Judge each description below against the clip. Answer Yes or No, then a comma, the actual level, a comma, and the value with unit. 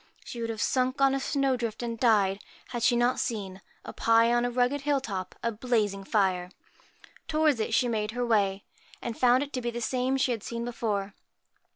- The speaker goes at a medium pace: No, fast, 210 wpm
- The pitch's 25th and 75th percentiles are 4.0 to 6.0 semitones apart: No, average, 2.9 semitones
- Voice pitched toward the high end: Yes, high, 235 Hz